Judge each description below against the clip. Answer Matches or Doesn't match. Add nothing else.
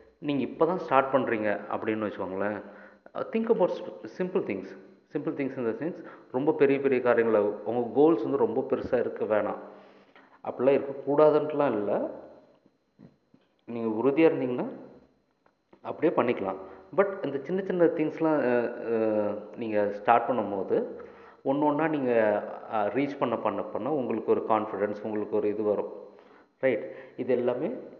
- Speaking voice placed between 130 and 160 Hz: Matches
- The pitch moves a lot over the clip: Matches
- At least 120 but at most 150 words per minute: Matches